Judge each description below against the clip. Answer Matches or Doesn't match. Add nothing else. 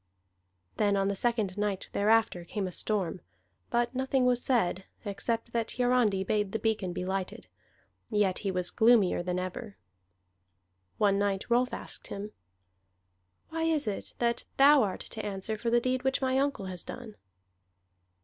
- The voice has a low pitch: Doesn't match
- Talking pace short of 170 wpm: Matches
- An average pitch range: Matches